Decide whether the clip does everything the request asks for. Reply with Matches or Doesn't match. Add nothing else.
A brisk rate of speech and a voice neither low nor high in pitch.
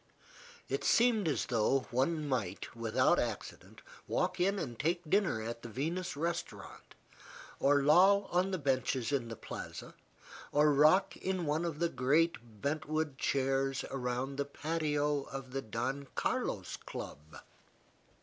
Doesn't match